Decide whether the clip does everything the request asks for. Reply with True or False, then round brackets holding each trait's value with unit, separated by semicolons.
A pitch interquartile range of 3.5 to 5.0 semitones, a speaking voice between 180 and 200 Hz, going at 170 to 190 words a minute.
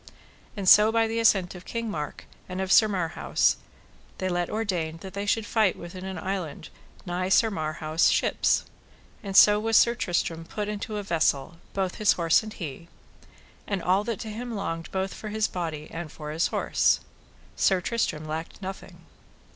True (4.1 semitones; 190 Hz; 180 wpm)